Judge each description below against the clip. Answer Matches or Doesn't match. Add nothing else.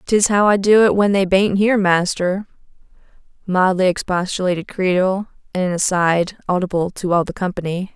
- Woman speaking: Matches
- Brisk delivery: Doesn't match